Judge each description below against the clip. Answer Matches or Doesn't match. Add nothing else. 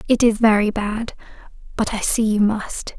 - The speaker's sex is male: Doesn't match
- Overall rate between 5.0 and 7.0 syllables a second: Doesn't match